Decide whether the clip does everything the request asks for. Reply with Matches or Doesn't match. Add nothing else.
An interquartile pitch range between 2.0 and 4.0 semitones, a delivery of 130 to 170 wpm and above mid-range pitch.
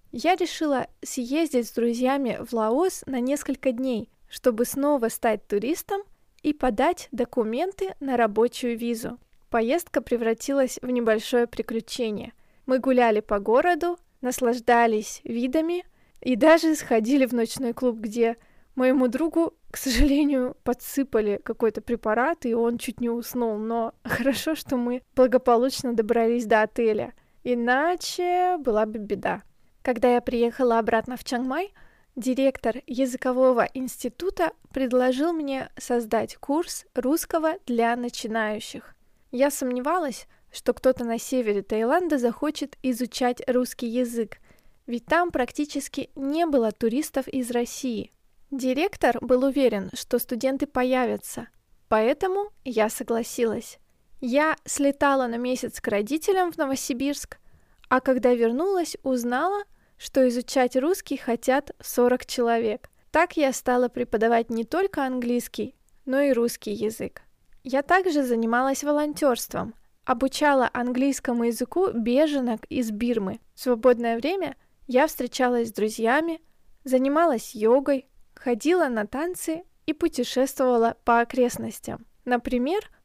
Doesn't match